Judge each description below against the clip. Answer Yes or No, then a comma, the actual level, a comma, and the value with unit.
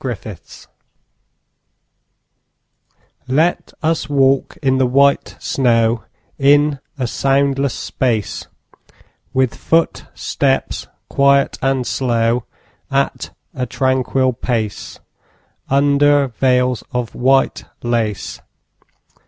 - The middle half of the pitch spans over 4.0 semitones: No, narrow, 2.4 semitones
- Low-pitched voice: Yes, low, 130 Hz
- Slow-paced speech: Yes, slow, 85 wpm